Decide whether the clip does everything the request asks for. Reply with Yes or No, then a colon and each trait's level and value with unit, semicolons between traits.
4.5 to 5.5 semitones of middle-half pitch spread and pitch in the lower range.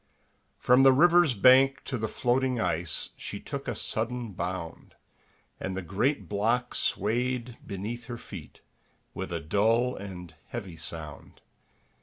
Yes: average, 5.2 semitones; low, 115 Hz